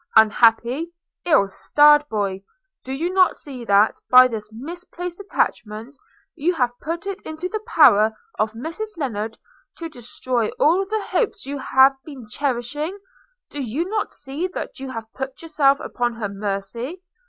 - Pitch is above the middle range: Yes, very high, 270 Hz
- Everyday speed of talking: Yes, average, 155 wpm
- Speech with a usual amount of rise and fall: No, wide, 6.5 semitones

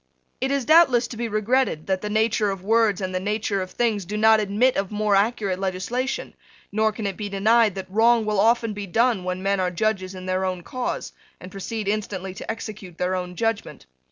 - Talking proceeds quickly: Yes, fast, 215 wpm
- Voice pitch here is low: No, high, 210 Hz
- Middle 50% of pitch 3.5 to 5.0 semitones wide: No, average, 3.1 semitones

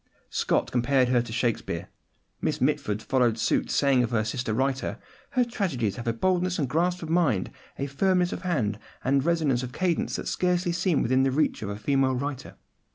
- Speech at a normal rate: Yes, average, 190 wpm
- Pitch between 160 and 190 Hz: No, low, 135 Hz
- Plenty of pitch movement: Yes, wide, 6.2 semitones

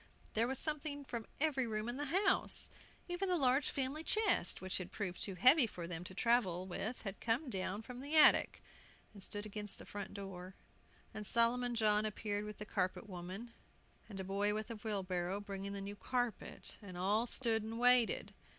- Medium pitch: No, high, 215 Hz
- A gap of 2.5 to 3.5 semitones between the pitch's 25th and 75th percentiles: No, average, 4.1 semitones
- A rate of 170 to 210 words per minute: Yes, average, 190 wpm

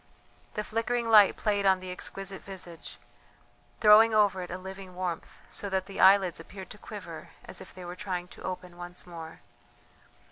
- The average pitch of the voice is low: No, high, 190 Hz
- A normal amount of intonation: No, narrow, 2.3 semitones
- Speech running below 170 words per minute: No, average, 175 wpm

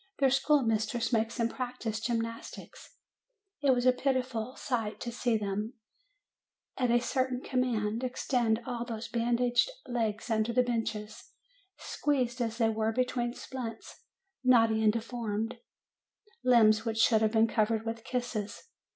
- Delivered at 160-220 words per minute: No, average, 140 wpm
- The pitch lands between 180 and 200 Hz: No, high, 235 Hz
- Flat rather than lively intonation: Yes, narrow, 2.0 semitones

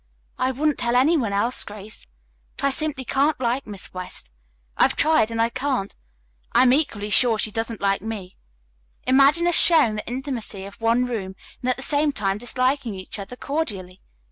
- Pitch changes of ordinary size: Yes, average, 4.8 semitones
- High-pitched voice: Yes, high, 240 Hz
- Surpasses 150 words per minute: Yes, average, 185 wpm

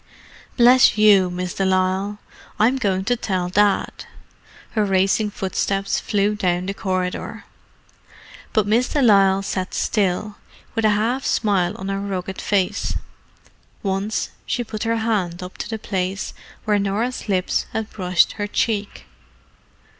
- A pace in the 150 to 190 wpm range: No, average, 140 wpm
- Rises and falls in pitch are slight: Yes, narrow, 2.3 semitones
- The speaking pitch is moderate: No, high, 200 Hz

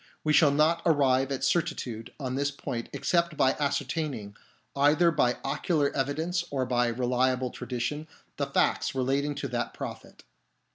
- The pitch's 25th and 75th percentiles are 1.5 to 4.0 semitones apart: Yes, average, 3.2 semitones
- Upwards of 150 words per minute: No, average, 145 wpm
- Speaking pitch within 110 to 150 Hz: Yes, medium, 140 Hz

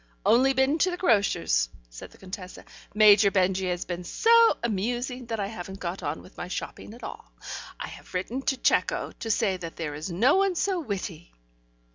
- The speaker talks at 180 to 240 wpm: Yes, average, 190 wpm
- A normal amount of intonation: No, wide, 6.1 semitones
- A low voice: No, high, 205 Hz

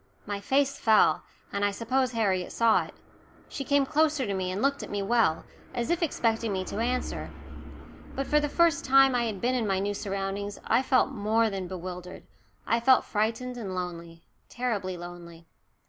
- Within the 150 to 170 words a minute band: No, average, 190 wpm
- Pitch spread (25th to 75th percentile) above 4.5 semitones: Yes, average, 5.0 semitones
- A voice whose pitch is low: No, high, 220 Hz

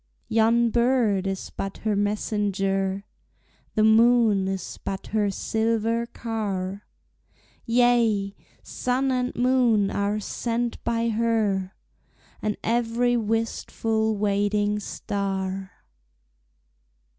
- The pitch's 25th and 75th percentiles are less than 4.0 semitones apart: Yes, narrow, 2.6 semitones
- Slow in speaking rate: Yes, slow, 90 wpm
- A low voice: No, high, 220 Hz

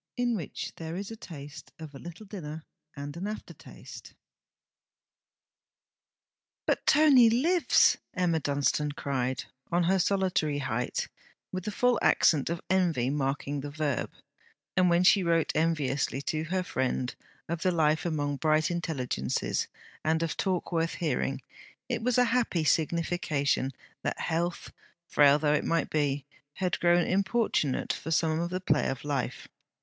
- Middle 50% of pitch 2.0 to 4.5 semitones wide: Yes, average, 4.1 semitones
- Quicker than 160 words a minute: No, average, 145 wpm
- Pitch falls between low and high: Yes, medium, 160 Hz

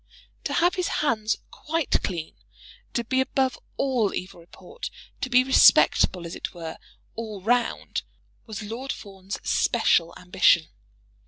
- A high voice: Yes, high, 220 Hz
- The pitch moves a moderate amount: No, wide, 6.1 semitones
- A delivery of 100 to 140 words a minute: Yes, slow, 135 wpm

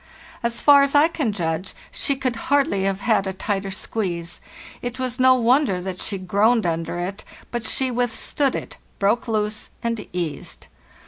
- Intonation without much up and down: No, average, 5.0 semitones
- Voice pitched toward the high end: Yes, high, 220 Hz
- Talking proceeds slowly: No, average, 170 wpm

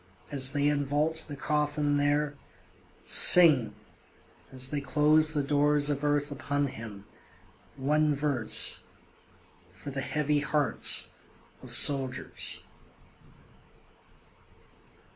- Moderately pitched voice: Yes, medium, 145 Hz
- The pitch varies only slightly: Yes, narrow, 1.4 semitones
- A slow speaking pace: Yes, slow, 95 wpm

